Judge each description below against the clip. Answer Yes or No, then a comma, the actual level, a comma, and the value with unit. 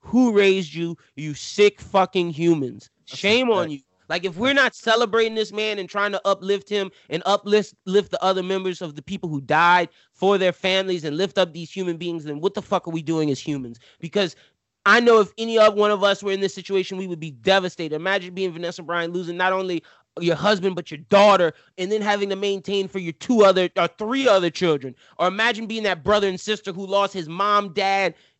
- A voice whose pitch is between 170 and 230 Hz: Yes, high, 190 Hz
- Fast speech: Yes, fast, 220 wpm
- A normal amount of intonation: Yes, average, 3.1 semitones